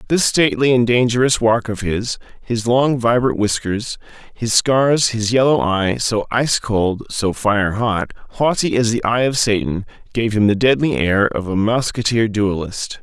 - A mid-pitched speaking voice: No, low, 115 Hz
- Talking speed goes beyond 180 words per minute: No, average, 170 wpm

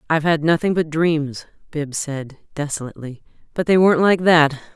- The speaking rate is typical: Yes, average, 165 wpm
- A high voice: No, medium, 155 Hz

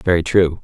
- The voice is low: Yes, very low, 85 Hz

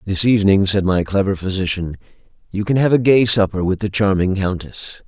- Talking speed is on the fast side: No, average, 190 wpm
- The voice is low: Yes, low, 100 Hz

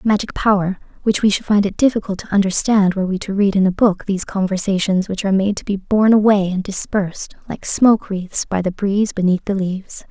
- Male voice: No, female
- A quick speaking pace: Yes, fast, 220 wpm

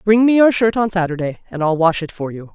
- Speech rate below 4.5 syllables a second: No, 6.0 syllables/s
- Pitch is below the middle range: No, medium, 185 Hz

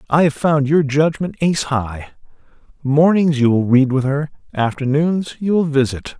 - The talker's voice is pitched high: No, medium, 145 Hz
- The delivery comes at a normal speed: Yes, average, 165 wpm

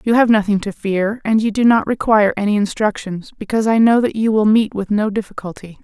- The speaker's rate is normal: No, fast, 225 wpm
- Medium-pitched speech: No, high, 210 Hz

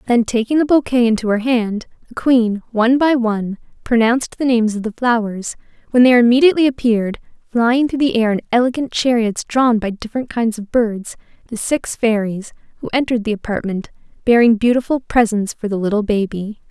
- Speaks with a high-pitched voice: Yes, high, 230 Hz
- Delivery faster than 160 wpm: Yes, average, 175 wpm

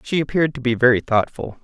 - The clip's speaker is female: No, male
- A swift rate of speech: Yes, fast, 220 wpm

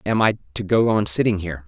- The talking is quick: Yes, fast, 250 wpm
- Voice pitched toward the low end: Yes, low, 100 Hz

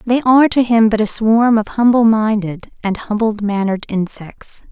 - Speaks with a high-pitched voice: Yes, high, 220 Hz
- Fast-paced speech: No, average, 180 wpm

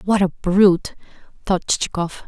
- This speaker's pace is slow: Yes, slow, 130 wpm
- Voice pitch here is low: No, medium, 185 Hz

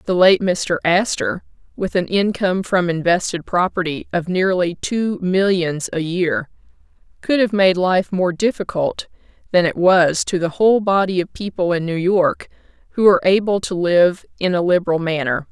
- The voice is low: No, medium, 180 Hz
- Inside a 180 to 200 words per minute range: No, average, 165 wpm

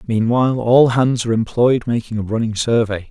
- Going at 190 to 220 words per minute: No, average, 175 wpm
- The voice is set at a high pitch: No, low, 115 Hz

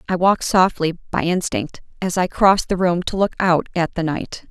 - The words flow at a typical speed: No, fast, 215 wpm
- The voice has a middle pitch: Yes, medium, 180 Hz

